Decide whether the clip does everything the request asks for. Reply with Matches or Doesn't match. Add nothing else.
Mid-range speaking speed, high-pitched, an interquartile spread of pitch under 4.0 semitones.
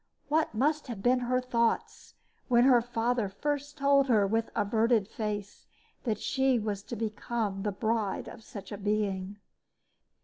Matches